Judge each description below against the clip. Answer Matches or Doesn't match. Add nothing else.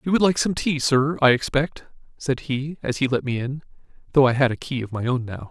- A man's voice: Matches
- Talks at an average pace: Doesn't match